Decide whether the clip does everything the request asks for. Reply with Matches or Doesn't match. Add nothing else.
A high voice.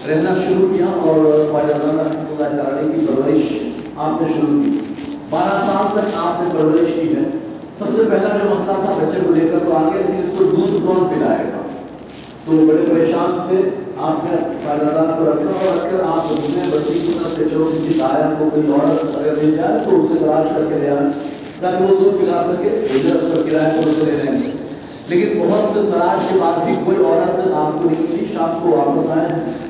Doesn't match